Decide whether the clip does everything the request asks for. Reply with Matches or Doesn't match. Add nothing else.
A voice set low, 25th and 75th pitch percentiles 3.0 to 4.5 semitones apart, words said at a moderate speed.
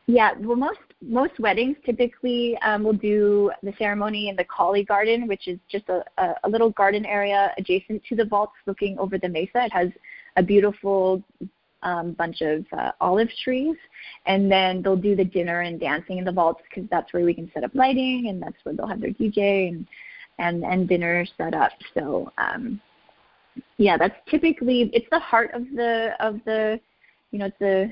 Doesn't match